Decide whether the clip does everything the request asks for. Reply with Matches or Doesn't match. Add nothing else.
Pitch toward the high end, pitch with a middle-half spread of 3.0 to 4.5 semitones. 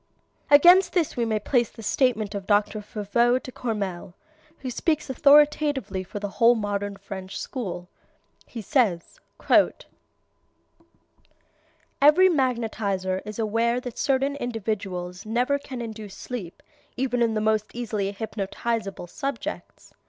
Matches